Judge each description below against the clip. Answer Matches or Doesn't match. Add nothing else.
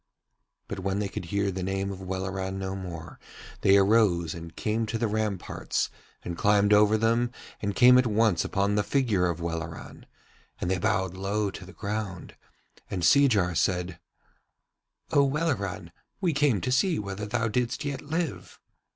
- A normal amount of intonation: Matches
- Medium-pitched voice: Doesn't match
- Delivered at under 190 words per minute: Matches